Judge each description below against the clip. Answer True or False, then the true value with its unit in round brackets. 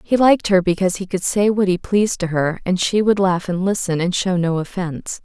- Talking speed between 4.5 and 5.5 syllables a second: False (5.7 syllables/s)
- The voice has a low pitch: False (185 Hz)